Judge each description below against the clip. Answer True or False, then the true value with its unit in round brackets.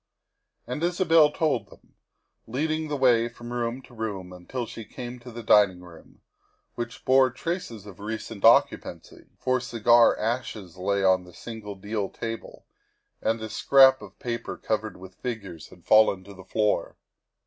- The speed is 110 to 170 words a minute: True (160 wpm)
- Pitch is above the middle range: False (115 Hz)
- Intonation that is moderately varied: True (4.0 semitones)